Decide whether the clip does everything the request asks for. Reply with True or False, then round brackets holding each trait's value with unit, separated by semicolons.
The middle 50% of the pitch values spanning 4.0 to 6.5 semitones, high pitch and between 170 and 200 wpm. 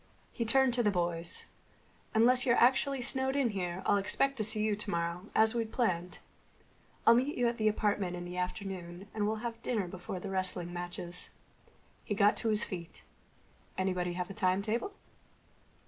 True (4.5 semitones; 205 Hz; 175 wpm)